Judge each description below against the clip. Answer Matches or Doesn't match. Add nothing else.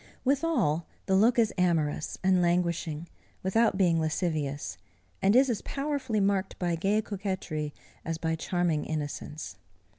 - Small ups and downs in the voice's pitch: Doesn't match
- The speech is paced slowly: Matches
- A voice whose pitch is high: Doesn't match